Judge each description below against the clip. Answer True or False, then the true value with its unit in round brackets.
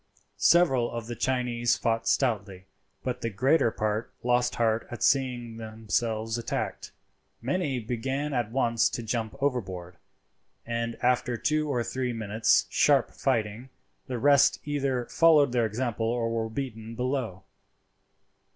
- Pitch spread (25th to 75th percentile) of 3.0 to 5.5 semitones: False (2.6 semitones)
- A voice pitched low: True (120 Hz)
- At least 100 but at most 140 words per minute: True (135 wpm)